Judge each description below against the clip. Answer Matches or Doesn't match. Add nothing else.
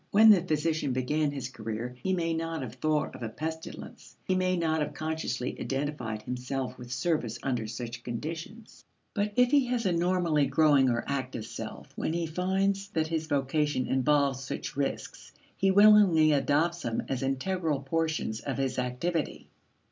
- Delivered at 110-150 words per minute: Doesn't match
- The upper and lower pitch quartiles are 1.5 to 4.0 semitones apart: Doesn't match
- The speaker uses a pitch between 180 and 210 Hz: Doesn't match